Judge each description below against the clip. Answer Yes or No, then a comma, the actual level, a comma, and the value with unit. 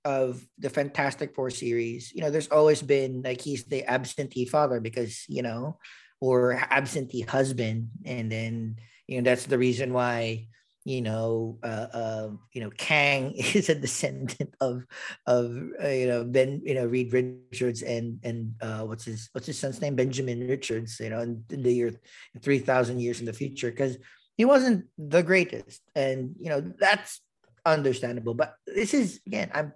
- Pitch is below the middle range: Yes, low, 125 Hz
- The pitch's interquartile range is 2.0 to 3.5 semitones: Yes, average, 2.9 semitones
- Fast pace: No, average, 175 wpm